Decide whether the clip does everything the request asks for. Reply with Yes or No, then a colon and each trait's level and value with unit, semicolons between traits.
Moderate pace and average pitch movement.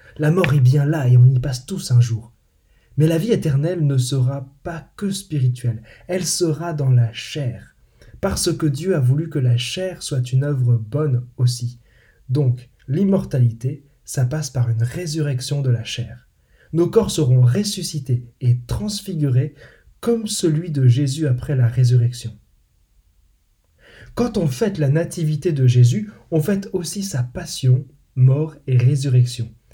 Yes: average, 155 wpm; average, 4.8 semitones